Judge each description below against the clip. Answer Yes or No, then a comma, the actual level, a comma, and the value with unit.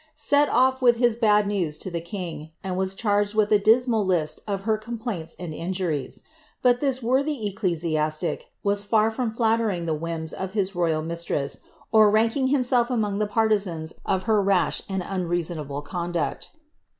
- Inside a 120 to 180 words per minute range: Yes, average, 175 wpm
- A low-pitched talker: No, high, 200 Hz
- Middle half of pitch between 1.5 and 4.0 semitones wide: No, average, 4.7 semitones